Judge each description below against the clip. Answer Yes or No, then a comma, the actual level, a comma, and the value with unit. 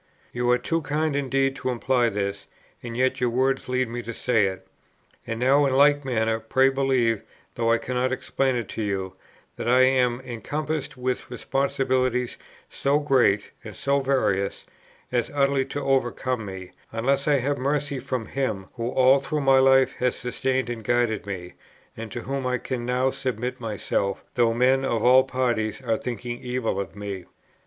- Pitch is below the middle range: Yes, low, 125 Hz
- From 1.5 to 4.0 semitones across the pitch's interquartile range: Yes, average, 2.7 semitones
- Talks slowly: No, average, 175 wpm